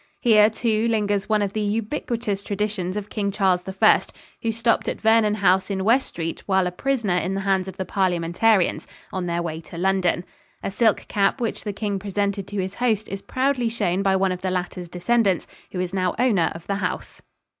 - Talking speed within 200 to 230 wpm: Yes, fast, 205 wpm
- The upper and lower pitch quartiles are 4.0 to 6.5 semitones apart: No, average, 2.8 semitones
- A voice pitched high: Yes, high, 200 Hz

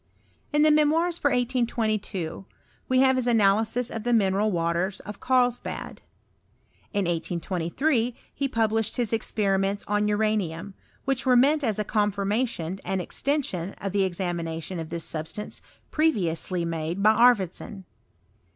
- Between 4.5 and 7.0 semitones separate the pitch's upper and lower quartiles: Yes, average, 5.0 semitones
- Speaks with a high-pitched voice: Yes, high, 210 Hz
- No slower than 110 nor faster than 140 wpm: Yes, slow, 135 wpm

